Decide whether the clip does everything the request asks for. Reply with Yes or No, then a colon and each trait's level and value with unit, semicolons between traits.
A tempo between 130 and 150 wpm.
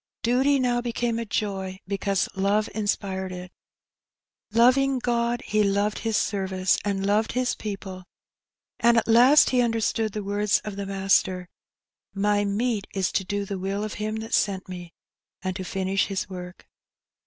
No: average, 160 wpm